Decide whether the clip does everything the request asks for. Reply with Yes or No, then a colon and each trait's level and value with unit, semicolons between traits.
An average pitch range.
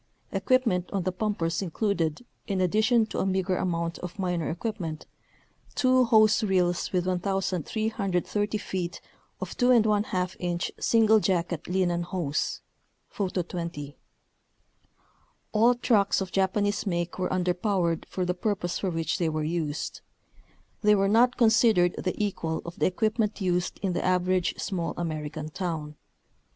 Yes: average, 3.3 semitones